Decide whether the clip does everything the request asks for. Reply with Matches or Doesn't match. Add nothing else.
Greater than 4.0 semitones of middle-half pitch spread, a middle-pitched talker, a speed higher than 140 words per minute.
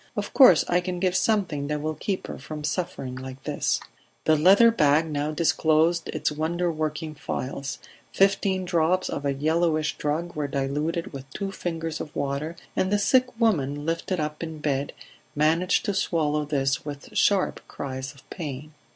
Doesn't match